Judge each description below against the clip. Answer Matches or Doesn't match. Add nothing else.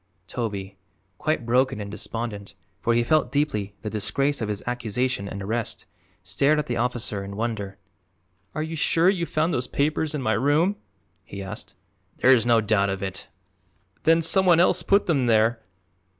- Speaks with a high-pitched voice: Doesn't match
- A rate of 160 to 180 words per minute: Matches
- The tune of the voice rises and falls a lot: Matches